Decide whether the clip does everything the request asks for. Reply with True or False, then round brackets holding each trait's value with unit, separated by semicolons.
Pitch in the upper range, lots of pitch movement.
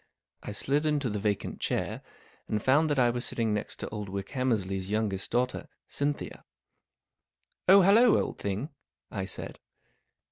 False (115 Hz; 5.8 semitones)